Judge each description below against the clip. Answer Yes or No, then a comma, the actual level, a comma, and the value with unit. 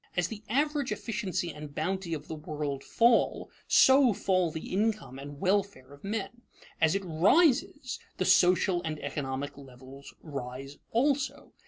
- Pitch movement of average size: No, wide, 7.8 semitones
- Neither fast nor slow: Yes, average, 145 wpm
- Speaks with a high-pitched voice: No, medium, 180 Hz